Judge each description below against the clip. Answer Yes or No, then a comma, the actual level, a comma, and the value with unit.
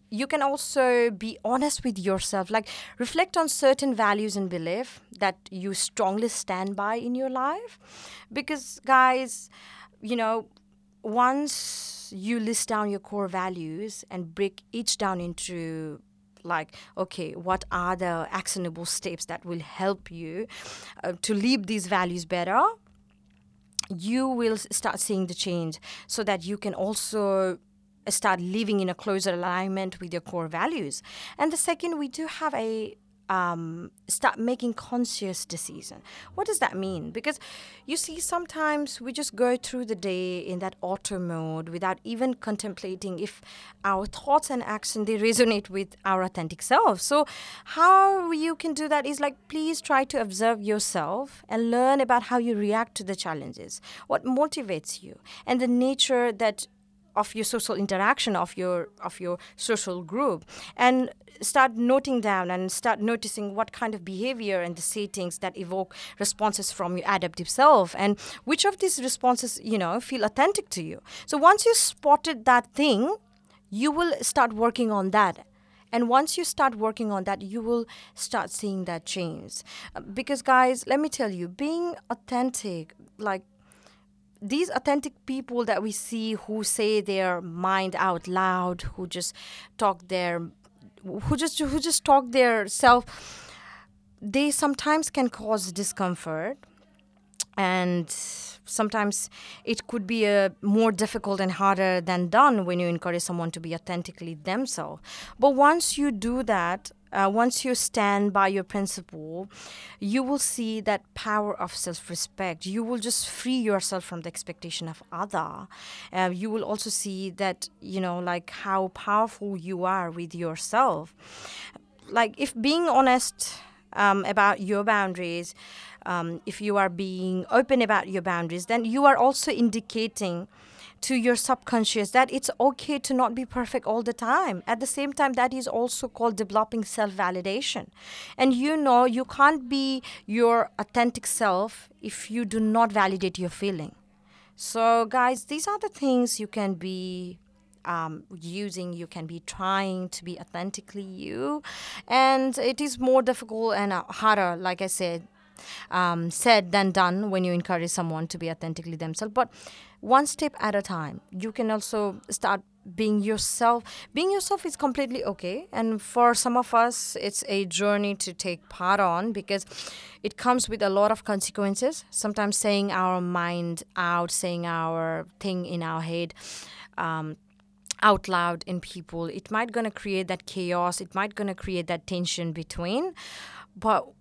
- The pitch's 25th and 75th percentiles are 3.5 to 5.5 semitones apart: Yes, average, 5.0 semitones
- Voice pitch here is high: Yes, high, 210 Hz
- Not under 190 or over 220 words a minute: No, average, 160 wpm